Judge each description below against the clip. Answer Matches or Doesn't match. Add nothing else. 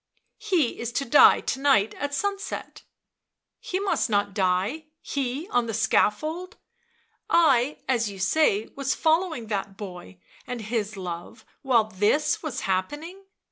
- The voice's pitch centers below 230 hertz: Doesn't match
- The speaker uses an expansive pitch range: Matches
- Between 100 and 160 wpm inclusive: Matches